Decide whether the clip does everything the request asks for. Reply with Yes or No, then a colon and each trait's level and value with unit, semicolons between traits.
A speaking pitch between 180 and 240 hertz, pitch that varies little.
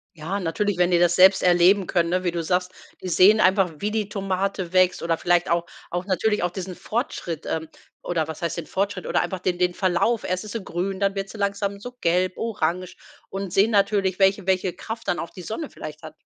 Yes: medium, 185 Hz; narrow, 2.3 semitones